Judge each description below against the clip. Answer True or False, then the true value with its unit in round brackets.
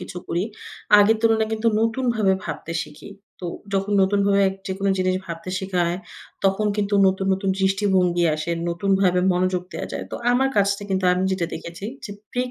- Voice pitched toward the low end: False (195 Hz)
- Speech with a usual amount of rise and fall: False (2.1 semitones)